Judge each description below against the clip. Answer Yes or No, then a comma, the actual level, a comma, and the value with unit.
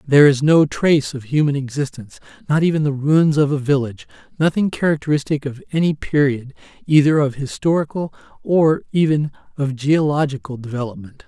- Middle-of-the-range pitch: Yes, medium, 145 Hz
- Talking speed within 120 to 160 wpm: Yes, average, 145 wpm